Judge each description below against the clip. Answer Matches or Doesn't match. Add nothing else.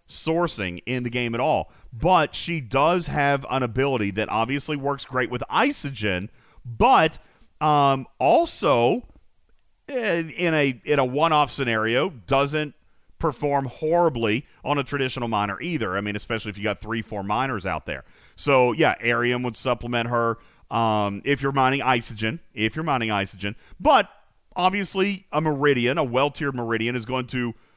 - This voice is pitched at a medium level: Doesn't match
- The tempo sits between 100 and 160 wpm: Matches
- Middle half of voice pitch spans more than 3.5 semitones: Matches